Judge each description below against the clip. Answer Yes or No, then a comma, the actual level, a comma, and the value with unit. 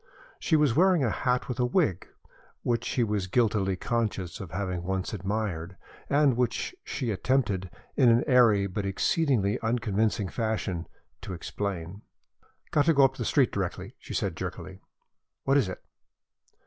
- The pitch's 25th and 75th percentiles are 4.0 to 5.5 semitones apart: Yes, average, 4.8 semitones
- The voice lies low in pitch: Yes, low, 110 Hz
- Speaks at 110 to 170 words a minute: Yes, average, 155 wpm